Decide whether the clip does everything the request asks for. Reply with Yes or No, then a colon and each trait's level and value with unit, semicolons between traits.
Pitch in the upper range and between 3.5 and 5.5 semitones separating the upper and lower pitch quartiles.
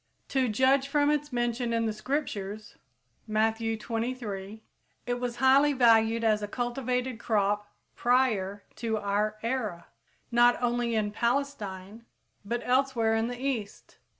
No: high, 230 Hz; average, 2.9 semitones